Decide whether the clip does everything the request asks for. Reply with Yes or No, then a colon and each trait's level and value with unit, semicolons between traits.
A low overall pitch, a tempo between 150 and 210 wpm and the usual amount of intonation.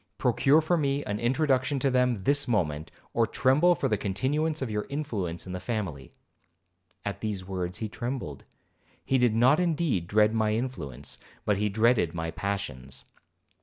No: low, 110 Hz; average, 165 wpm; wide, 6.2 semitones